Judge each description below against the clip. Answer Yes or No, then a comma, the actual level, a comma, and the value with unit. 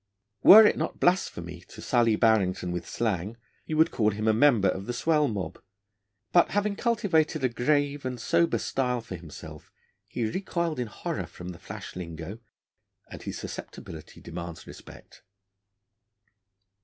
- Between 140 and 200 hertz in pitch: No, low, 115 Hz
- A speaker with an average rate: Yes, average, 150 wpm